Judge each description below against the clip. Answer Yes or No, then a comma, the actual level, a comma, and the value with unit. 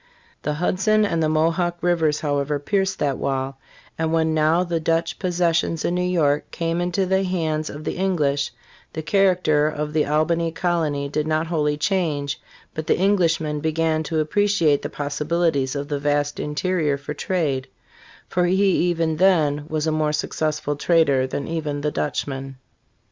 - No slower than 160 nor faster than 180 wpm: Yes, average, 170 wpm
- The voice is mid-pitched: Yes, medium, 155 Hz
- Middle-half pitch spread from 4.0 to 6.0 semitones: No, average, 2.8 semitones